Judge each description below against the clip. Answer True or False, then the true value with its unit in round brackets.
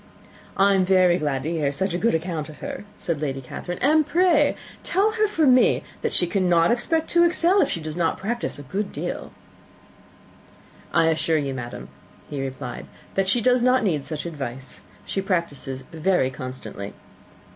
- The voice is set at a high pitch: False (175 Hz)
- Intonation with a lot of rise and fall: True (8.5 semitones)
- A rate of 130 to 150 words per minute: False (180 wpm)